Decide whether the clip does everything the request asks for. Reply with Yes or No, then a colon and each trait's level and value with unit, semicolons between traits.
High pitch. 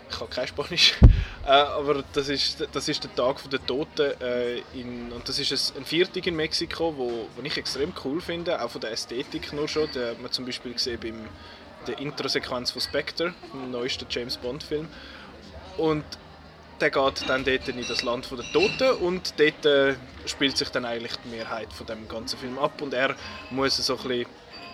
No: low, 130 Hz